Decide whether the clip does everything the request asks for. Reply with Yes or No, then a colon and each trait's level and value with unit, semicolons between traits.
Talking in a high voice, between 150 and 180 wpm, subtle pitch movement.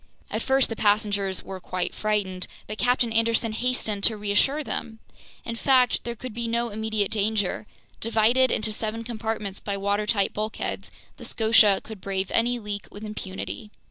Yes: high, 215 Hz; average, 160 wpm; narrow, 2.1 semitones